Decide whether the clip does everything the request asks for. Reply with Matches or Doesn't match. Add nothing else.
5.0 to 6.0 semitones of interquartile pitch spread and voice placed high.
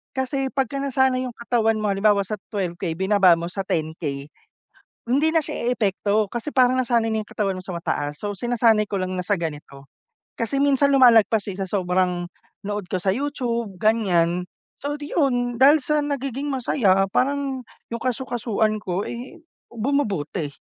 Matches